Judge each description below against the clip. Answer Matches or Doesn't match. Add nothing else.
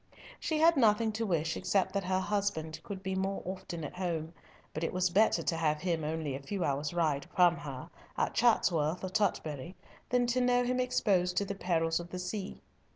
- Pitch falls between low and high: Matches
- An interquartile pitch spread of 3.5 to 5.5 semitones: Matches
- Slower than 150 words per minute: Doesn't match